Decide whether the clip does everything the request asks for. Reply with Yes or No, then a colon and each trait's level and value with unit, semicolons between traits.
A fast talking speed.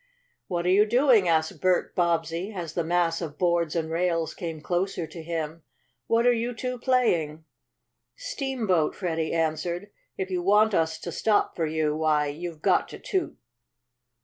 No: average, 165 wpm